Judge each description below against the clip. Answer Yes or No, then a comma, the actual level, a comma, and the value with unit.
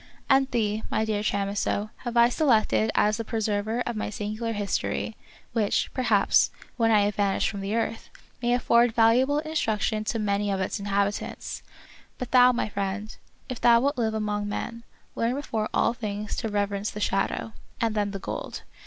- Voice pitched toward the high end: Yes, high, 215 Hz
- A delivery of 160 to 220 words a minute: Yes, average, 180 wpm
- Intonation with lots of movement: No, narrow, 2.4 semitones